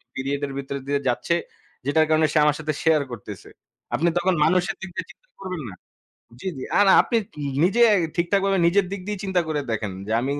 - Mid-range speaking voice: Yes, medium, 160 Hz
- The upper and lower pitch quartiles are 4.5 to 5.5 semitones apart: Yes, average, 5.2 semitones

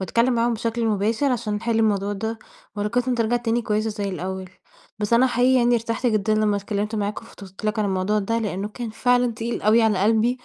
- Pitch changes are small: Yes, narrow, 2.2 semitones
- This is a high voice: Yes, high, 220 Hz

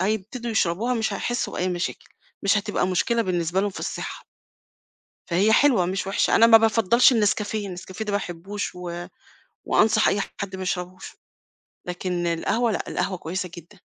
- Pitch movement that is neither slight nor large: Yes, average, 3.4 semitones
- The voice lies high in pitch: Yes, high, 195 Hz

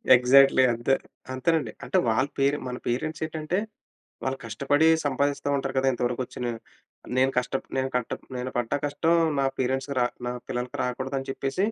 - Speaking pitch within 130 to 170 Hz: Yes, low, 135 Hz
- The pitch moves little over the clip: Yes, narrow, 2.2 semitones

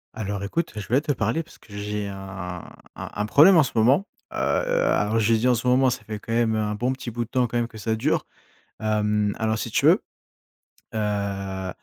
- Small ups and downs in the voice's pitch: No, average, 3.1 semitones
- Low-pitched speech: Yes, low, 110 Hz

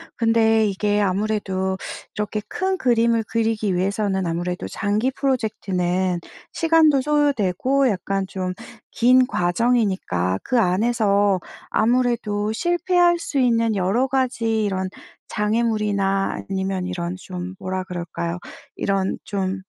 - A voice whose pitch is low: No, high, 210 Hz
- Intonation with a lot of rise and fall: No, average, 4.0 semitones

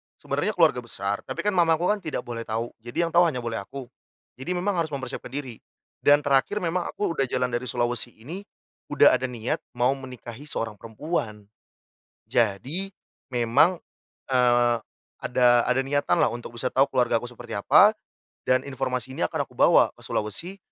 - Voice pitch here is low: Yes, low, 130 Hz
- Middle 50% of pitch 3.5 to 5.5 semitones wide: Yes, average, 4.7 semitones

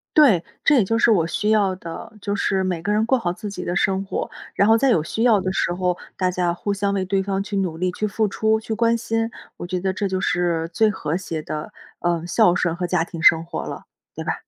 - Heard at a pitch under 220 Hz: Yes, high, 190 Hz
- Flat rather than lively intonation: No, average, 3.3 semitones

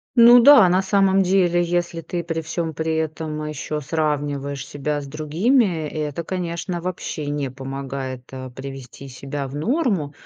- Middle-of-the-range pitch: Yes, medium, 155 Hz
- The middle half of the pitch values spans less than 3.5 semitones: No, average, 3.8 semitones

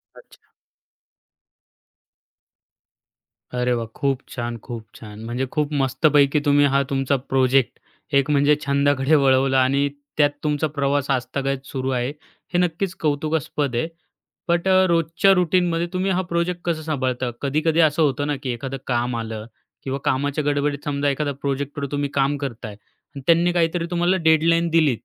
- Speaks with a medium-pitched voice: Yes, medium, 145 Hz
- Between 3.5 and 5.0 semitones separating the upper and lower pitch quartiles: No, average, 3.1 semitones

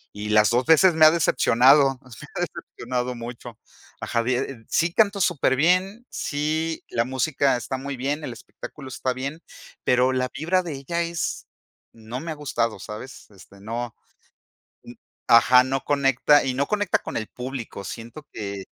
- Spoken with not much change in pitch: No, average, 4.3 semitones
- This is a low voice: Yes, low, 130 Hz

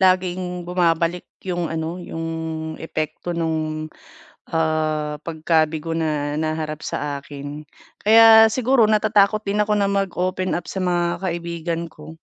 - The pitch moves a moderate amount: Yes, average, 3.0 semitones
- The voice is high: No, medium, 170 Hz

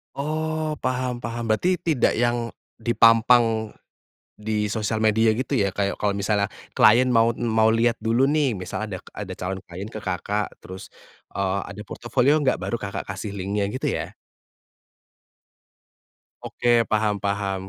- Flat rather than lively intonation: No, average, 3.0 semitones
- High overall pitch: No, low, 110 Hz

